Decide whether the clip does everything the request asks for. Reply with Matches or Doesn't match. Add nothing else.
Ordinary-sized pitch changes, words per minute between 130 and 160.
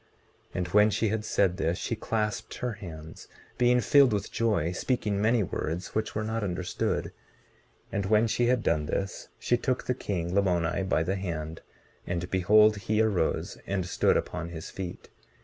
Doesn't match